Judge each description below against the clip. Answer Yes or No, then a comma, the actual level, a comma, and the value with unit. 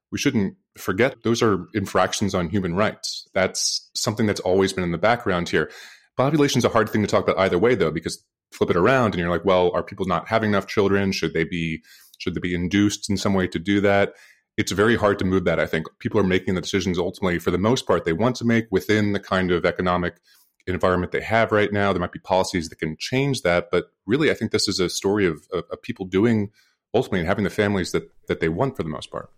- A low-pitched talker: Yes, very low, 95 Hz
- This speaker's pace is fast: Yes, fast, 245 wpm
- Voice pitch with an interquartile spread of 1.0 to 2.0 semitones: No, average, 2.7 semitones